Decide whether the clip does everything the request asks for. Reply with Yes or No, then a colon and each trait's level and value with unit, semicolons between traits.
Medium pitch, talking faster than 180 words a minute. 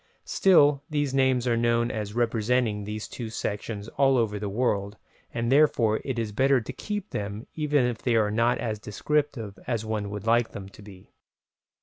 No: low, 115 Hz; average, 190 wpm